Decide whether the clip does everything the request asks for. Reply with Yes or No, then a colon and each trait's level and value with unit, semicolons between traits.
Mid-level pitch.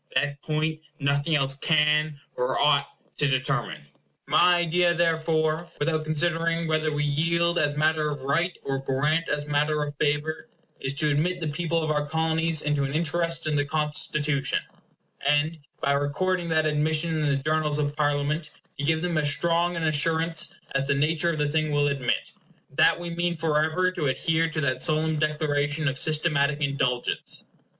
Yes: medium, 155 Hz